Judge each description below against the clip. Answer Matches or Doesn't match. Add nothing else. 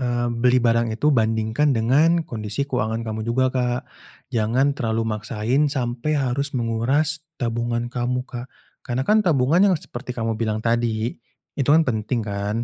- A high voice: Doesn't match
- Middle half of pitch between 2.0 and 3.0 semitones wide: Matches